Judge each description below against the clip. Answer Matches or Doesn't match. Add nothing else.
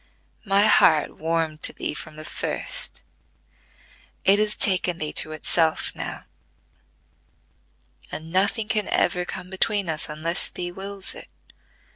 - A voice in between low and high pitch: Matches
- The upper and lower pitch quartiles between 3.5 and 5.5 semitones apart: Matches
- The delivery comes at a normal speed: Doesn't match